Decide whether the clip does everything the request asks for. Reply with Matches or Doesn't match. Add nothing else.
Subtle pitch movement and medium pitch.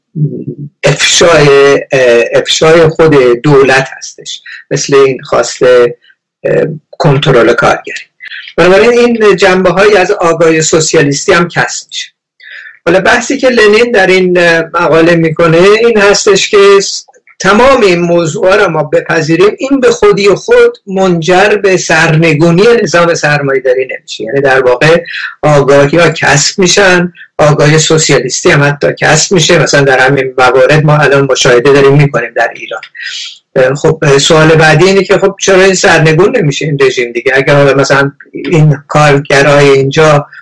Doesn't match